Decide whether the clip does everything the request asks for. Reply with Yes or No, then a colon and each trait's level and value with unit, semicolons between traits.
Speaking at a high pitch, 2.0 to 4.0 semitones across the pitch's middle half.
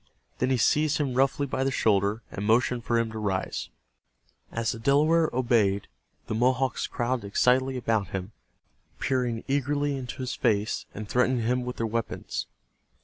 No: low, 125 Hz; average, 2.9 semitones